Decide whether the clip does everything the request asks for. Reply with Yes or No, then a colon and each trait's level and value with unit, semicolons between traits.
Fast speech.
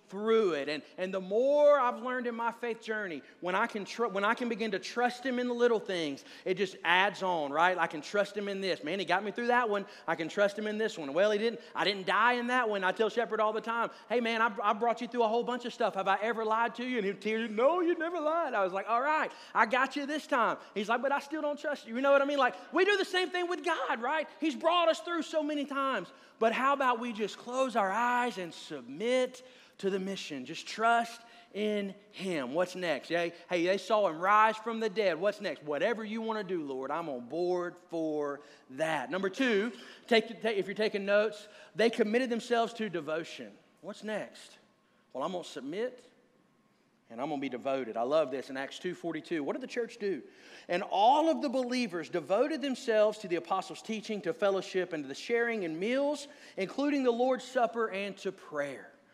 Yes: fast, 235 wpm